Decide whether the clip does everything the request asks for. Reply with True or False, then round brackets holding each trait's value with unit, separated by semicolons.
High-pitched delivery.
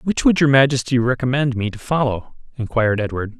False (125 Hz)